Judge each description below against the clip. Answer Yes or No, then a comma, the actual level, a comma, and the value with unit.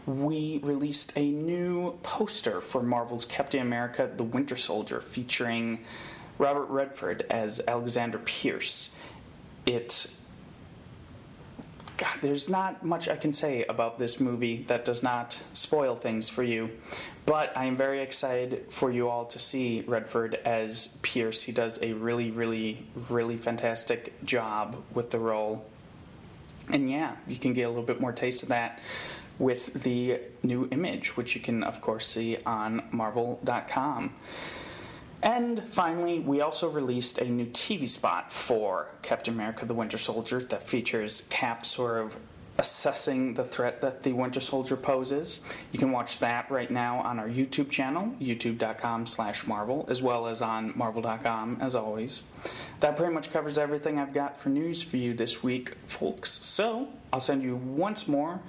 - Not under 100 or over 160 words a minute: Yes, average, 155 wpm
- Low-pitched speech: Yes, low, 125 Hz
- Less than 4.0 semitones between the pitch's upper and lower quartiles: Yes, average, 3.5 semitones